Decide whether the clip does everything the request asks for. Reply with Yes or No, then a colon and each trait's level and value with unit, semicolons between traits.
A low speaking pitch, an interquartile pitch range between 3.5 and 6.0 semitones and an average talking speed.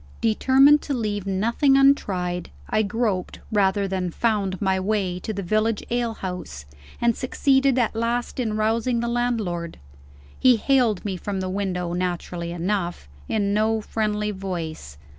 No: high, 210 Hz; average, 4.0 semitones; average, 145 wpm